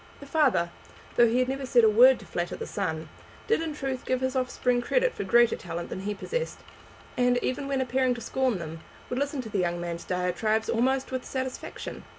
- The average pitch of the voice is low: No, very high, 250 Hz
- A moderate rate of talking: No, fast, 210 wpm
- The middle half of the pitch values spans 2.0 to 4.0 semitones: No, average, 4.9 semitones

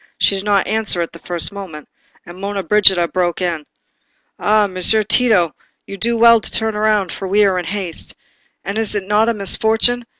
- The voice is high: Yes, high, 200 Hz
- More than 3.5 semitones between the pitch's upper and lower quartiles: No, average, 3.0 semitones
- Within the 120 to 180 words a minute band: No, average, 195 wpm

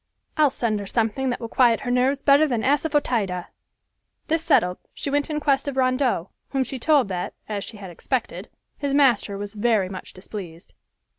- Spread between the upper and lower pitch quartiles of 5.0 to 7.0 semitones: Yes, wide, 5.4 semitones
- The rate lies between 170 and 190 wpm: Yes, average, 180 wpm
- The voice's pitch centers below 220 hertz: No, very high, 250 Hz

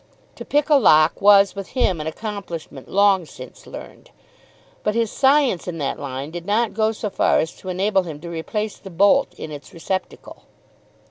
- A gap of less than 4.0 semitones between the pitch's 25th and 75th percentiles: No, average, 4.8 semitones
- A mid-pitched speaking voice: No, high, 195 Hz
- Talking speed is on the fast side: No, average, 185 wpm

